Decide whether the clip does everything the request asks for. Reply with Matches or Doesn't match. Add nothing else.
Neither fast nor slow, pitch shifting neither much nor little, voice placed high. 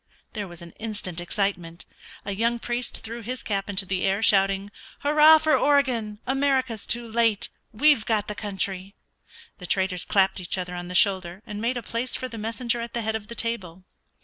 Matches